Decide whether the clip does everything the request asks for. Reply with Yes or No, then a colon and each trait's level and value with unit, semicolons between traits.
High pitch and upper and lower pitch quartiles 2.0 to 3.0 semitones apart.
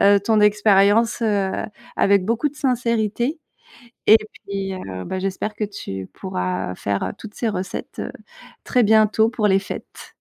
Yes: high, 205 Hz; narrow, 2.6 semitones